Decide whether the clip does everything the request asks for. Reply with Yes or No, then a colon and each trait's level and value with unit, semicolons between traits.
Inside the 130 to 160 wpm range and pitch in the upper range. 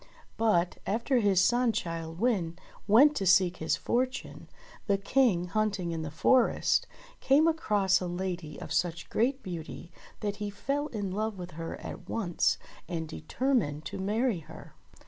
Yes: average, 155 wpm; high, 195 Hz